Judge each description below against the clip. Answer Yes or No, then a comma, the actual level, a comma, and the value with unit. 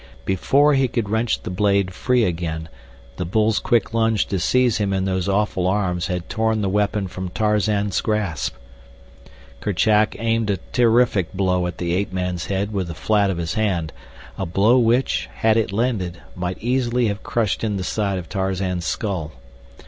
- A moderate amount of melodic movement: Yes, average, 3.4 semitones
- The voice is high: No, low, 100 Hz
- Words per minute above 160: Yes, average, 175 wpm